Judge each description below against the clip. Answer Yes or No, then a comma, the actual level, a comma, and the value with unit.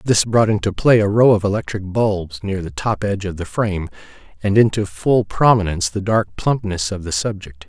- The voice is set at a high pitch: No, low, 100 Hz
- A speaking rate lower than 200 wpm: No, fast, 205 wpm